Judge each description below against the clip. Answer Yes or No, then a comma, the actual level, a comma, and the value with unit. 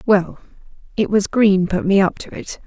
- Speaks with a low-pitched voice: No, high, 195 Hz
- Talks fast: No, average, 180 wpm